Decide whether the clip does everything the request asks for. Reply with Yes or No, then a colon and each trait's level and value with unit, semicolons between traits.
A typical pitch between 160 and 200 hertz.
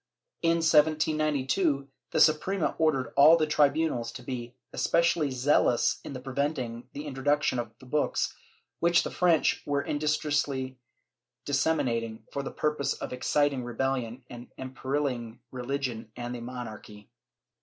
No: low, 135 Hz